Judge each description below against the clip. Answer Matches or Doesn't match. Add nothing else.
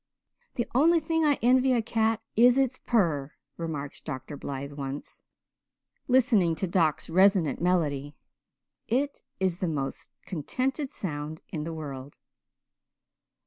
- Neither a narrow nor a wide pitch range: Doesn't match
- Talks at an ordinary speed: Doesn't match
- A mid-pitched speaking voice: Matches